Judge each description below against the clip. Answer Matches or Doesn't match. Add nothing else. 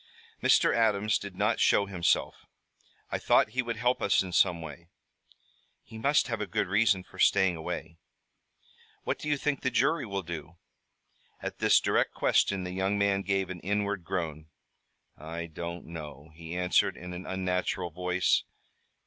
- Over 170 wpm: Doesn't match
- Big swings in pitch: Doesn't match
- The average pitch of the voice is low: Matches